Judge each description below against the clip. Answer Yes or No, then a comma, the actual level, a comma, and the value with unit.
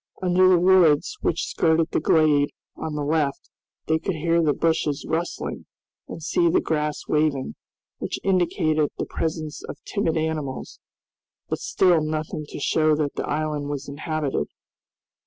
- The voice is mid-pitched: Yes, medium, 155 Hz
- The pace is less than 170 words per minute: Yes, average, 150 wpm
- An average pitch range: No, narrow, 1.9 semitones